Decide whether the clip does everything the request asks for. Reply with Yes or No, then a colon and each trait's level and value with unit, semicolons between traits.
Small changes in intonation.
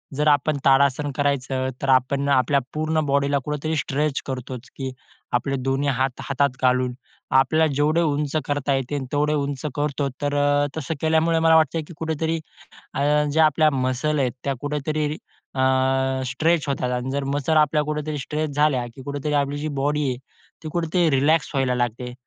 Yes: narrow, 2.3 semitones